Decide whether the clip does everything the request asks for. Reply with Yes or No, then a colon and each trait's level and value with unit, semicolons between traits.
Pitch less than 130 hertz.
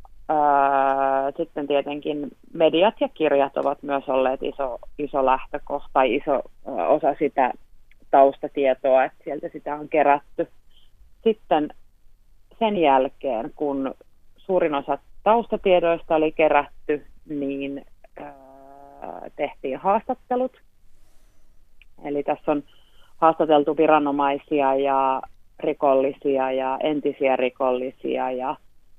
No: medium, 140 Hz